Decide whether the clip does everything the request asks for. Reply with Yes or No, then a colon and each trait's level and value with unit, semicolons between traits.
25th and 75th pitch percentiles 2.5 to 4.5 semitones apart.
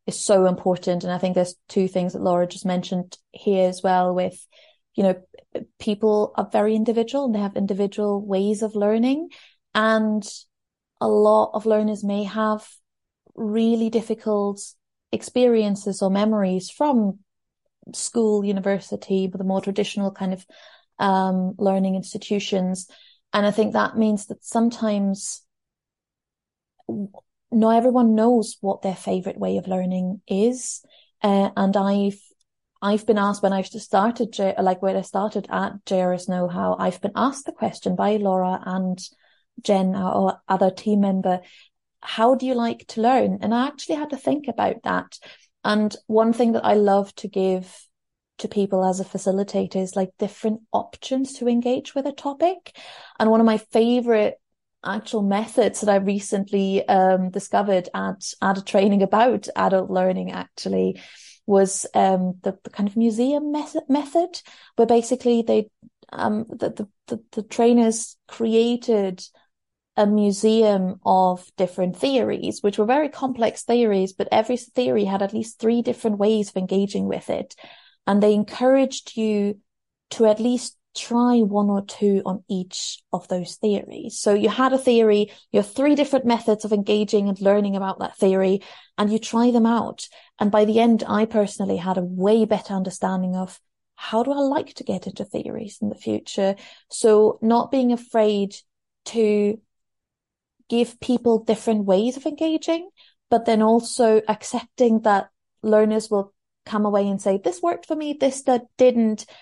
Yes: average, 3.1 semitones